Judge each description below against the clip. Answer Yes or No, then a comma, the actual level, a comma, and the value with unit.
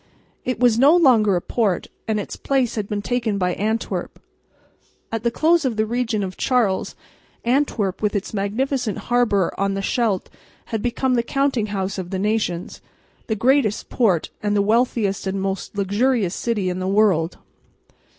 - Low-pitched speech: No, high, 215 Hz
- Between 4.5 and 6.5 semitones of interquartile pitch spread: No, average, 3.8 semitones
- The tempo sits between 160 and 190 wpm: Yes, average, 170 wpm